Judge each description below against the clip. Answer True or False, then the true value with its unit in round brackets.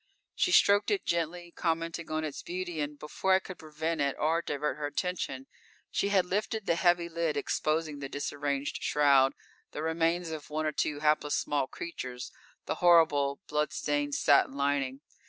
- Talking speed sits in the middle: True (170 wpm)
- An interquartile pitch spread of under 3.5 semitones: True (2.9 semitones)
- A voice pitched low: False (155 Hz)